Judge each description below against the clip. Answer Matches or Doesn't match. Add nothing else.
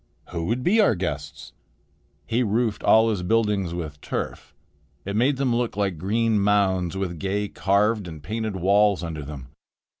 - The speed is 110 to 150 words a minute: Doesn't match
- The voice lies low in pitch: Matches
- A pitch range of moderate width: Matches